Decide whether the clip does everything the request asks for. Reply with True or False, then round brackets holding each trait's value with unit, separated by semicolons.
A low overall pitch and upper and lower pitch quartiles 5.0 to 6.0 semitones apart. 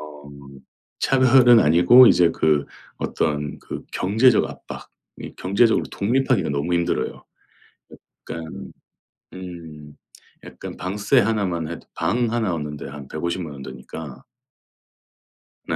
False (85 Hz; 6.8 semitones)